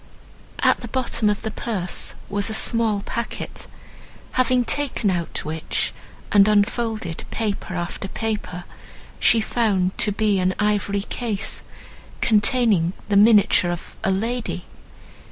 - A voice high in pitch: Yes, high, 210 Hz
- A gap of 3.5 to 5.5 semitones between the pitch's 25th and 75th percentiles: No, average, 3.1 semitones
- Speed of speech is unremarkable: No, slow, 120 wpm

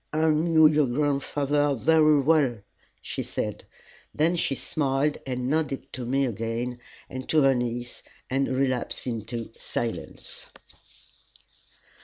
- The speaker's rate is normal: No, slow, 120 wpm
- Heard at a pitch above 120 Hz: Yes, low, 135 Hz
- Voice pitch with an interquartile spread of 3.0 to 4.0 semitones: Yes, average, 3.5 semitones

